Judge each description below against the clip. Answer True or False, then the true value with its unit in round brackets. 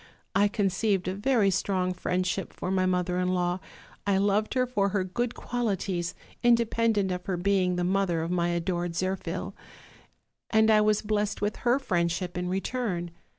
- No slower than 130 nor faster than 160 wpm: False (170 wpm)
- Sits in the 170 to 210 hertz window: True (190 Hz)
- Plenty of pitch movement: False (2.7 semitones)